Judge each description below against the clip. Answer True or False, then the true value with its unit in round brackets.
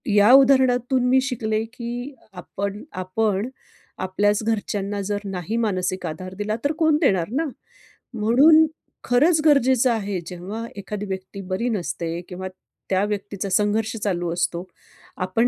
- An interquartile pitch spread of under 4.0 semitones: False (4.5 semitones)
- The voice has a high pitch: True (210 Hz)